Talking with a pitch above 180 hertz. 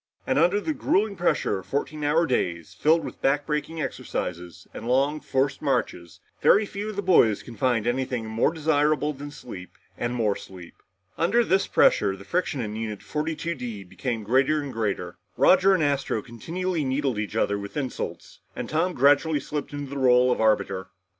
No: low, 135 Hz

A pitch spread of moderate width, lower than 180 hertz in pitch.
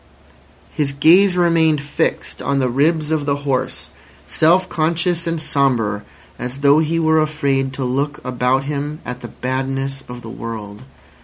Yes: average, 3.4 semitones; medium, 140 Hz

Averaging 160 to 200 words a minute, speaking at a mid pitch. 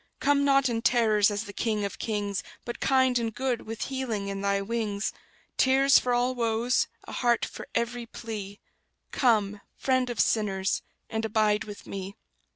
No: average, 165 wpm; high, 225 Hz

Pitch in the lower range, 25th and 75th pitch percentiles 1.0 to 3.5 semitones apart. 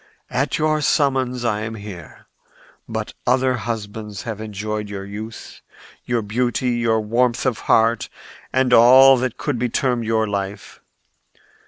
Yes: low, 115 Hz; average, 2.9 semitones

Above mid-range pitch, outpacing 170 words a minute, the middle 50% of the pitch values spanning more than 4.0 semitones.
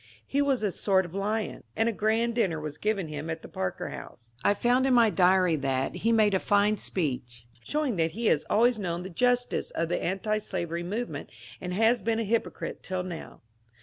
Yes: high, 200 Hz; fast, 205 wpm; average, 5.1 semitones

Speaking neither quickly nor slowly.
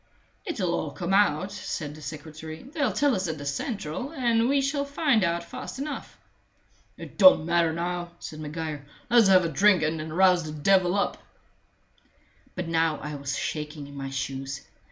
Yes: average, 175 wpm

